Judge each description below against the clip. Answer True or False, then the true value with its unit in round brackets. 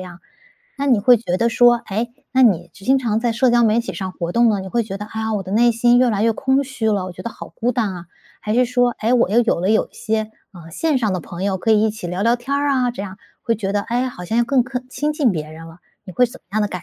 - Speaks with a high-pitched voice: True (225 Hz)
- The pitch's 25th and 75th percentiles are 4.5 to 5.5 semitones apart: False (4.0 semitones)